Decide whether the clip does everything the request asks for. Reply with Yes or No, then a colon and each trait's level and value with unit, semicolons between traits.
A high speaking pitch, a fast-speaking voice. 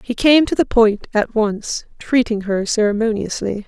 No: high, 220 Hz; average, 165 wpm